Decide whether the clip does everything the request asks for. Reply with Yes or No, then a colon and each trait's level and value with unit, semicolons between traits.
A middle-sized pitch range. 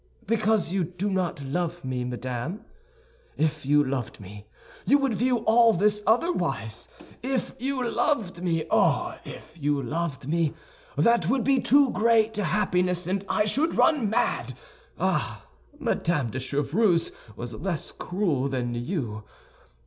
No: wide, 8.2 semitones